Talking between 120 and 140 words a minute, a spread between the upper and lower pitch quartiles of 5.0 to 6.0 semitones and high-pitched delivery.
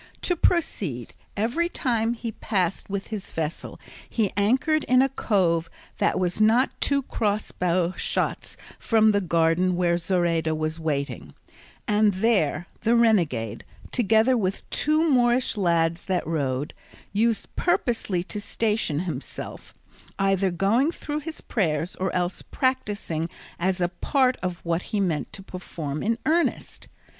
Yes: slow, 135 wpm; wide, 5.5 semitones; high, 195 Hz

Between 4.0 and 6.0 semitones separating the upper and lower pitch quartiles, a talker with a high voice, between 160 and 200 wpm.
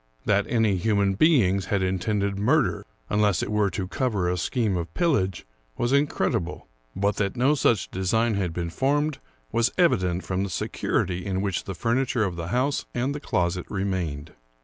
No: average, 4.5 semitones; low, 100 Hz; average, 175 wpm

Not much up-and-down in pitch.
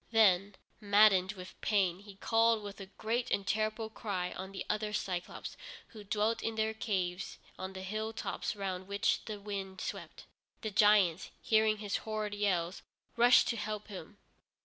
Yes: narrow, 2.2 semitones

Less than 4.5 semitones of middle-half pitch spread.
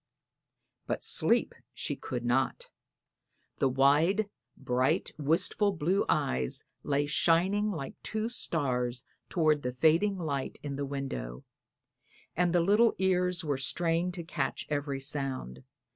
No: average, 5.0 semitones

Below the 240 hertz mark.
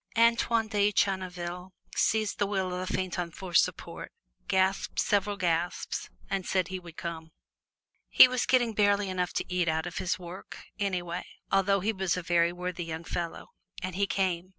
Yes: medium, 185 Hz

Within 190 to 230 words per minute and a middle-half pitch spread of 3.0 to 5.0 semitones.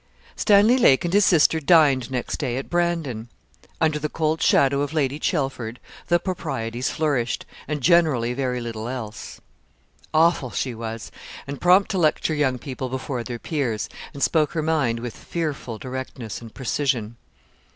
No: average, 155 wpm; average, 4.7 semitones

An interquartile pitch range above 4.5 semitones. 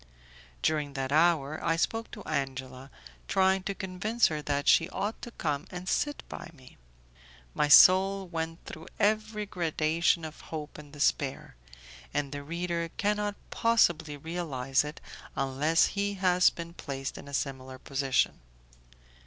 Yes: average, 4.9 semitones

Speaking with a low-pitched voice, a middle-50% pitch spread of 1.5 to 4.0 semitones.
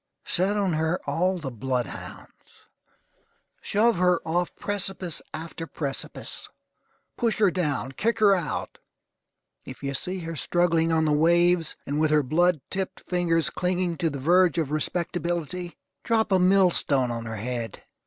No: medium, 170 Hz; average, 3.4 semitones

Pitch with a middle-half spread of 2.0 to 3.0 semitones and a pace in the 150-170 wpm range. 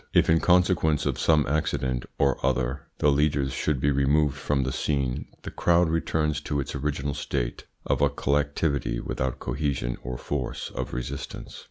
Yes: narrow, 2.5 semitones; average, 165 wpm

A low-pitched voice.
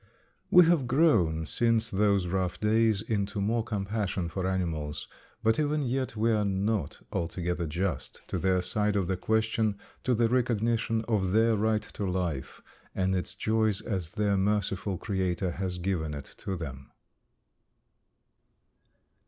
Yes: low, 100 Hz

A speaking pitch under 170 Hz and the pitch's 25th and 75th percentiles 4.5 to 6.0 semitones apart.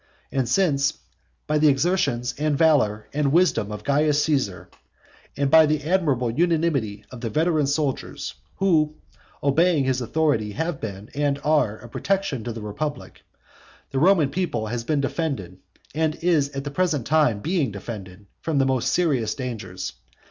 Yes: medium, 140 Hz; average, 5.2 semitones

